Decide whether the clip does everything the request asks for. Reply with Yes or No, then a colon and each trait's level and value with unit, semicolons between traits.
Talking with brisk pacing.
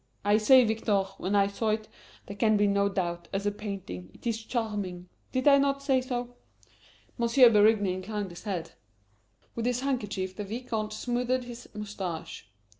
No: average, 170 wpm